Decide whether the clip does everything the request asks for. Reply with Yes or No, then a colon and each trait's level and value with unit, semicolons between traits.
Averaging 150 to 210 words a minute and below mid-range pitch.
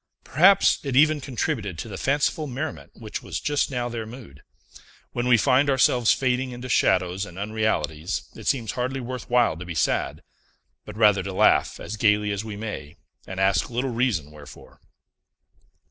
Yes: average, 170 wpm; low, 115 Hz